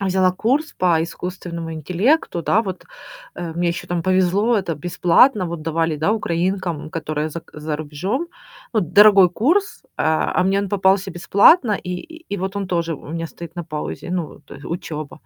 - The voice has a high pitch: No, medium, 180 Hz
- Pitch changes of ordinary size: Yes, average, 3.3 semitones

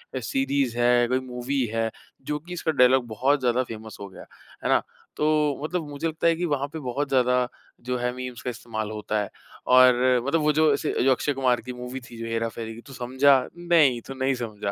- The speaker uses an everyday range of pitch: Yes, average, 3.0 semitones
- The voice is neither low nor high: No, low, 130 Hz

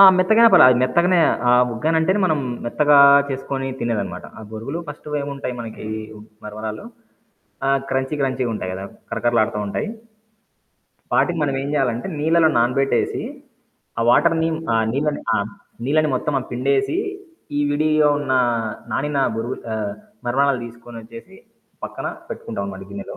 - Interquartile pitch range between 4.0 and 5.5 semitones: Yes, average, 4.4 semitones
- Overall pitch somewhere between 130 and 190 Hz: Yes, low, 135 Hz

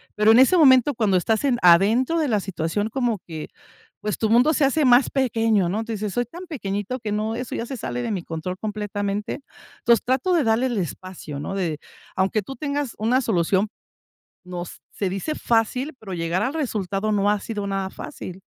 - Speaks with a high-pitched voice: Yes, high, 215 Hz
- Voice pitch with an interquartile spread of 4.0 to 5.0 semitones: Yes, average, 4.5 semitones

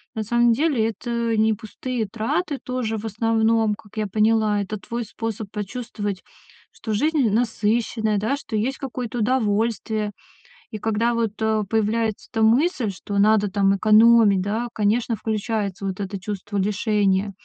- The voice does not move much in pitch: Yes, narrow, 2.0 semitones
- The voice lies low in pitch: No, high, 220 Hz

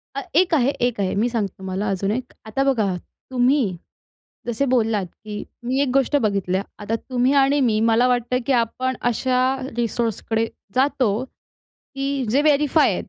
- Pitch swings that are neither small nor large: Yes, average, 4.0 semitones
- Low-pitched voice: No, high, 245 Hz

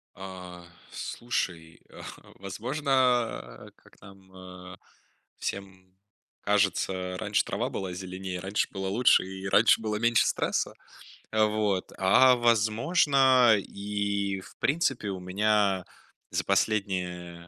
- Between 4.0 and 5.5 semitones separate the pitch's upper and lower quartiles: No, average, 3.2 semitones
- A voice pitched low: Yes, low, 100 Hz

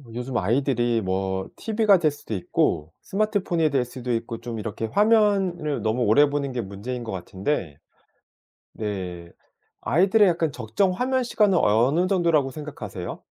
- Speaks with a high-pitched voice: No, low, 130 Hz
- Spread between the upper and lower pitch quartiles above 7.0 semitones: Yes, wide, 8.4 semitones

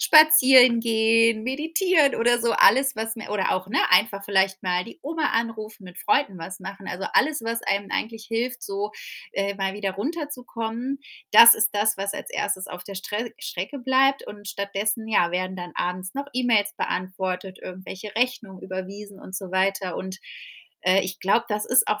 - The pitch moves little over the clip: No, average, 3.8 semitones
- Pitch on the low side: No, high, 210 Hz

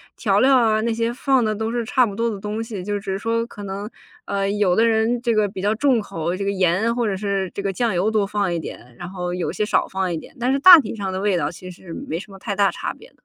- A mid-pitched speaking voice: No, high, 205 Hz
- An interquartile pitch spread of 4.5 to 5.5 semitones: No, average, 3.2 semitones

